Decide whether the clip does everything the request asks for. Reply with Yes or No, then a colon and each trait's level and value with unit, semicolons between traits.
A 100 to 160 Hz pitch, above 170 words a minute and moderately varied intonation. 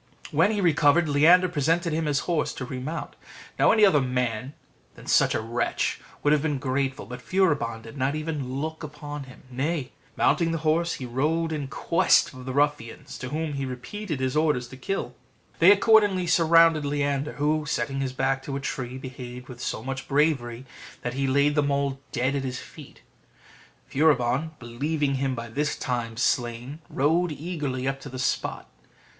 Yes: medium, 140 Hz; average, 180 wpm; average, 3.5 semitones